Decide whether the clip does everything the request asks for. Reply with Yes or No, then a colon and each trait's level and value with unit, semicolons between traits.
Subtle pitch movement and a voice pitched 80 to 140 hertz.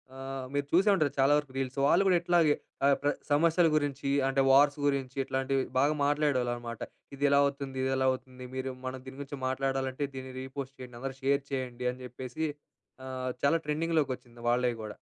Yes: narrow, 1.9 semitones; low, 135 Hz